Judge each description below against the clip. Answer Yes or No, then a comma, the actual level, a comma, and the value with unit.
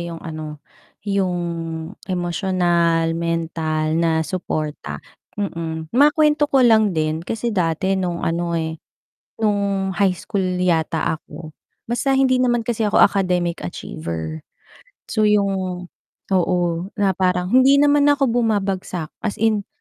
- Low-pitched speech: No, medium, 185 Hz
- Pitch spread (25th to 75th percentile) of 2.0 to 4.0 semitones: No, average, 4.5 semitones